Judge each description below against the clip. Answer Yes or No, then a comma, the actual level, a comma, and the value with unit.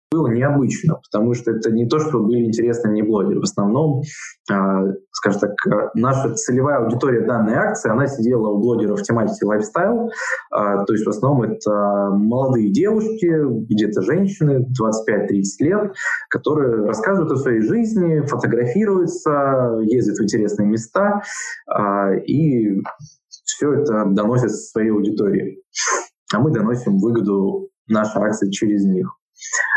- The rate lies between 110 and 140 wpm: Yes, average, 125 wpm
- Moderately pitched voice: No, low, 115 Hz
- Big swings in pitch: Yes, wide, 6.9 semitones